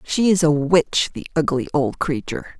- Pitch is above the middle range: No, medium, 155 Hz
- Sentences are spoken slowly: No, average, 185 wpm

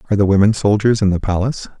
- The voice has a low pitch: Yes, low, 100 Hz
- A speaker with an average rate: No, fast, 235 wpm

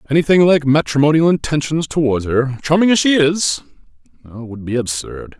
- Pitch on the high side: No, medium, 145 Hz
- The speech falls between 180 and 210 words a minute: No, average, 145 wpm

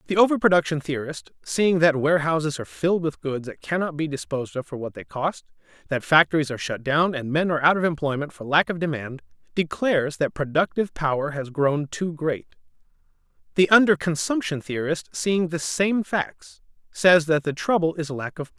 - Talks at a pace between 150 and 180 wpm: No, average, 195 wpm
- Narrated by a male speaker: Yes, male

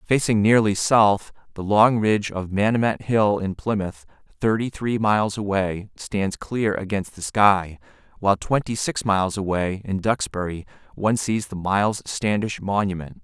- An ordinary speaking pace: Yes, average, 150 wpm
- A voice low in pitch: Yes, low, 100 Hz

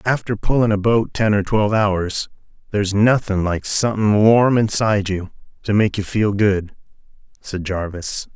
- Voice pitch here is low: Yes, low, 105 Hz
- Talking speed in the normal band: Yes, average, 160 wpm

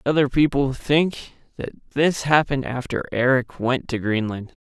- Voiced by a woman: No, male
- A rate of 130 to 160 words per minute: Yes, average, 140 wpm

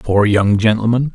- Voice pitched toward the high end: No, low, 110 Hz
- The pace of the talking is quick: No, average, 160 wpm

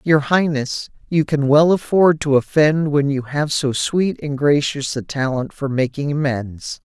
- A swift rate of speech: No, average, 175 wpm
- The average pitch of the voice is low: No, medium, 145 Hz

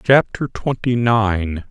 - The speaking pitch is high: No, low, 110 Hz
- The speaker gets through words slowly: Yes, slow, 105 wpm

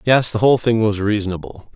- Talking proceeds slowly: No, fast, 205 wpm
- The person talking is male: Yes, male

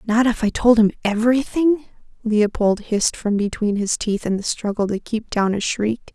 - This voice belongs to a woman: Yes, female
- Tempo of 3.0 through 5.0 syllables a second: Yes, 4.9 syllables/s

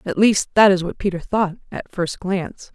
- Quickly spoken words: Yes, fast, 220 wpm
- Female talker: Yes, female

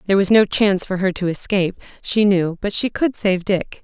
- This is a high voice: Yes, high, 195 Hz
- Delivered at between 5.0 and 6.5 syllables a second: Yes, 5.6 syllables/s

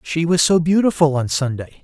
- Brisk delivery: No, average, 195 wpm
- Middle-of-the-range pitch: Yes, medium, 160 Hz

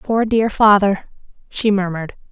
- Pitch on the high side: Yes, high, 205 Hz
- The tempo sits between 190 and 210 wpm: No, slow, 130 wpm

